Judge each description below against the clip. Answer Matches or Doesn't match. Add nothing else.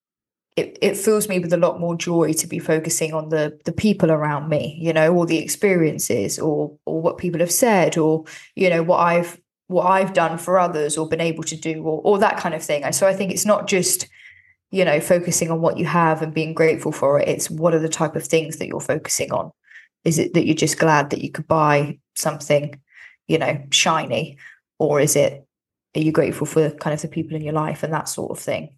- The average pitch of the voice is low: Doesn't match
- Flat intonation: Matches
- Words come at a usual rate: Doesn't match